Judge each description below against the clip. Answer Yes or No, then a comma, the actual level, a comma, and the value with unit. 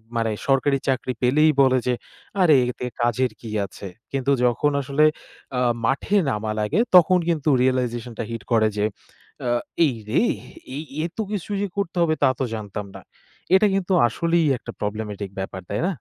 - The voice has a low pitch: Yes, low, 130 Hz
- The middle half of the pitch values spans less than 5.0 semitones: No, wide, 5.6 semitones